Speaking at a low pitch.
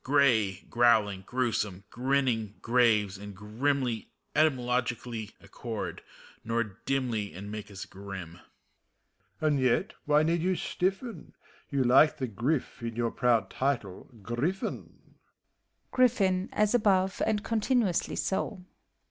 Yes: low, 120 Hz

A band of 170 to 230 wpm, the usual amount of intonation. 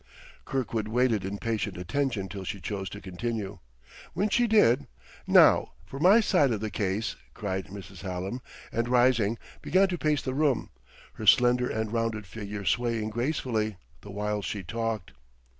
No: average, 160 wpm; average, 3.9 semitones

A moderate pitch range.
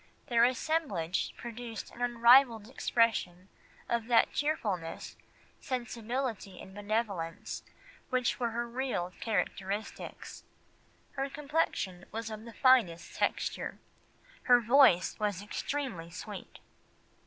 Yes: average, 4.1 semitones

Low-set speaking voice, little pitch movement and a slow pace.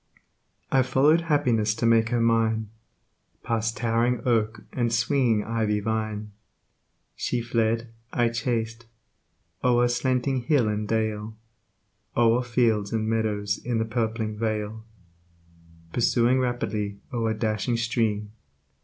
Yes: low, 115 Hz; narrow, 1.9 semitones; slow, 115 wpm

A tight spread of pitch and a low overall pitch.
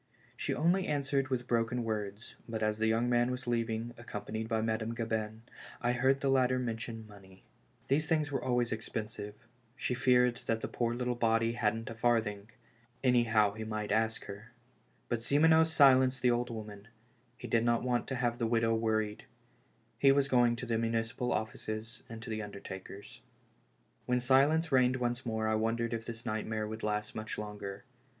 Yes: narrow, 2.1 semitones; low, 115 Hz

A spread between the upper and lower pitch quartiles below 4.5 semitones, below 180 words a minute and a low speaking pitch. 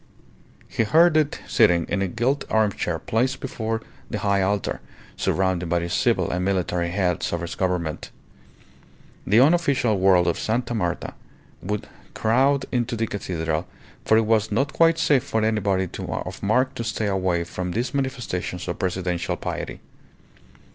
No: average, 5.0 semitones; average, 155 wpm; low, 105 Hz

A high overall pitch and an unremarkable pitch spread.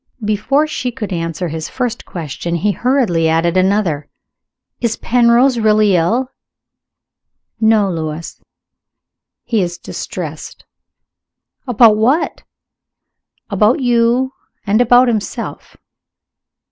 No: high, 215 Hz; wide, 6.0 semitones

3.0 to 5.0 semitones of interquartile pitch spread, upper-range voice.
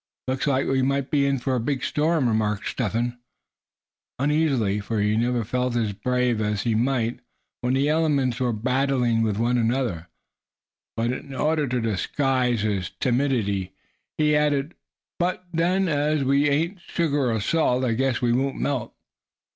No: average, 3.7 semitones; low, 125 Hz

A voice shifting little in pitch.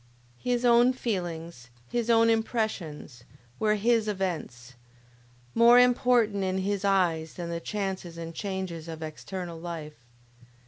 No: wide, 5.4 semitones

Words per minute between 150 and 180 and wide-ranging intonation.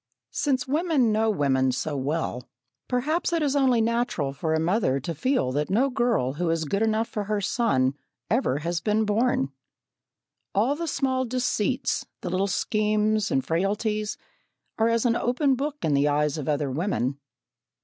Yes: average, 170 wpm; wide, 8.5 semitones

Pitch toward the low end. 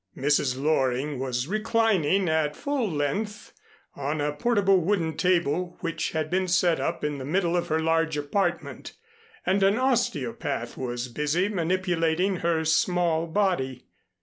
No: medium, 165 Hz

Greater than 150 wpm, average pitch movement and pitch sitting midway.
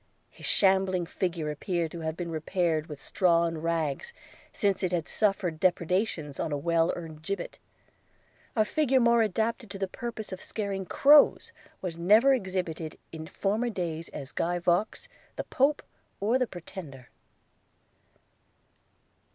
No: average, 145 wpm; average, 4.2 semitones; medium, 180 Hz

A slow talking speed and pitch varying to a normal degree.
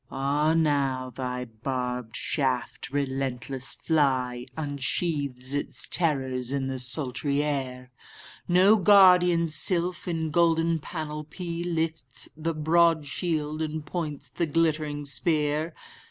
Yes: slow, 110 wpm; average, 3.7 semitones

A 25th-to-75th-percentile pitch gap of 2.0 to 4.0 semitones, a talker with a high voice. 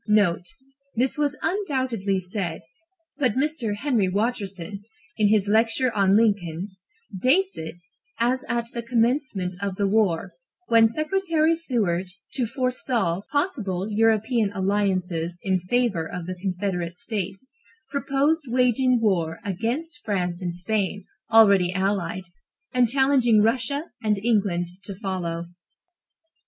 No: average, 5.1 semitones; high, 210 Hz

